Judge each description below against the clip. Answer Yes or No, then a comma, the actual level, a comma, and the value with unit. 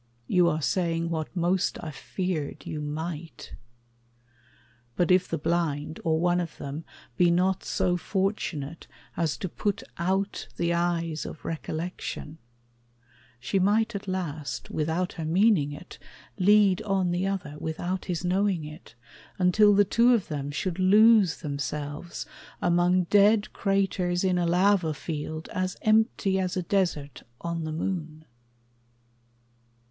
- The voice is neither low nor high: Yes, medium, 175 Hz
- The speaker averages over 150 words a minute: No, slow, 135 wpm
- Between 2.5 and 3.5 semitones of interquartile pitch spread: Yes, average, 3.2 semitones